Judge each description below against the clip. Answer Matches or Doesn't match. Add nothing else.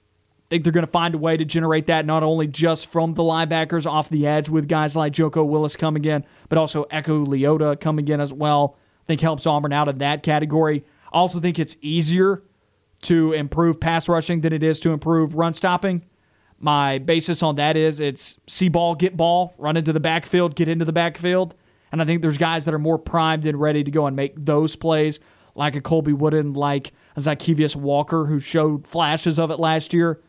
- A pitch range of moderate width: Doesn't match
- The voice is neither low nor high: Matches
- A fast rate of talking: Matches